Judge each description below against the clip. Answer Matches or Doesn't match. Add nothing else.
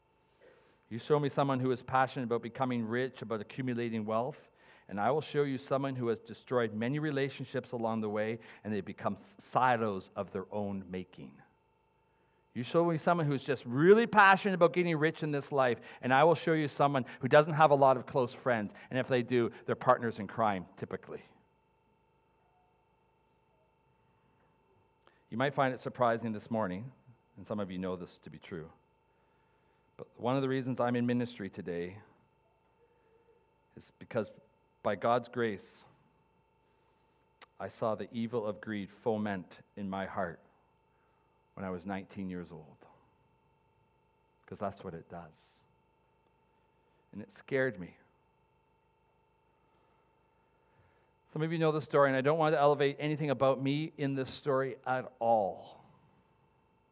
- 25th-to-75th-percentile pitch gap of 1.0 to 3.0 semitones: Doesn't match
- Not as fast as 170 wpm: Matches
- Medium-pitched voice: Doesn't match